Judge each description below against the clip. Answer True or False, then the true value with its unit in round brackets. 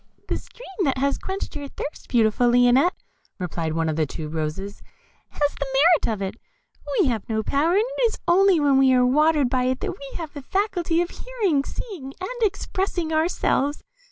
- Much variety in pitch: True (6.5 semitones)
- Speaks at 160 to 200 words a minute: True (190 wpm)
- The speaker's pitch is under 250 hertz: False (285 Hz)